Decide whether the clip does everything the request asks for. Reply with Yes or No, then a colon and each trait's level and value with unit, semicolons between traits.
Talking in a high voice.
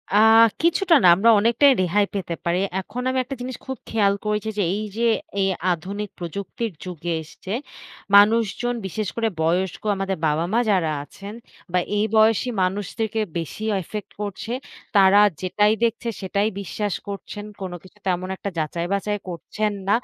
Yes: high, 205 Hz